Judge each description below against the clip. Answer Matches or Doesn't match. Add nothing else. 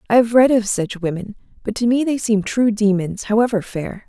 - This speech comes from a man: Doesn't match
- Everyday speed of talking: Doesn't match